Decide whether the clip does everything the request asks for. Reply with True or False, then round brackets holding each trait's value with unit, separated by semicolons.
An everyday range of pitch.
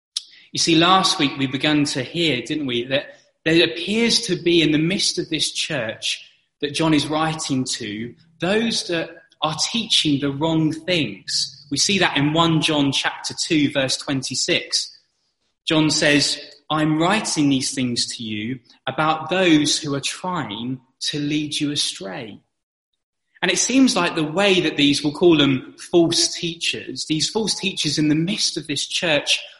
True (3.3 semitones)